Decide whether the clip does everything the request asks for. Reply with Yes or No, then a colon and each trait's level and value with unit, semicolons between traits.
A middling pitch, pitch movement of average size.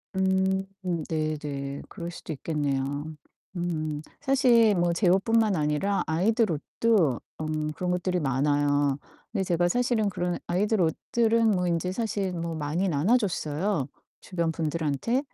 Yes: medium, 175 Hz; average, 4.9 semitones